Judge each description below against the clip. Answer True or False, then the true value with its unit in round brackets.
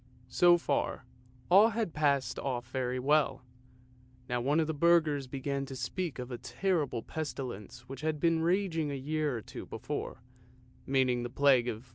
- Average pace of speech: True (170 wpm)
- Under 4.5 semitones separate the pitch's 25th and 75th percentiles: True (4.1 semitones)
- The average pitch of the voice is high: False (140 Hz)